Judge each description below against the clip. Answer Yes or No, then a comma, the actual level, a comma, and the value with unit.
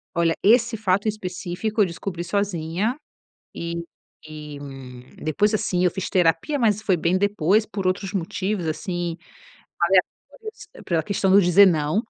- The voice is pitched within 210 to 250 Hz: No, medium, 185 Hz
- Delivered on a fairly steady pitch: No, average, 3.7 semitones